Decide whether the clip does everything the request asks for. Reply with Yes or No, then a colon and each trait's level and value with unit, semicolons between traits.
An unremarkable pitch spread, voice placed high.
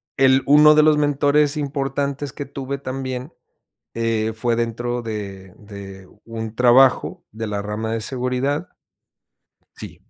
No: average, 3.9 semitones; low, 125 Hz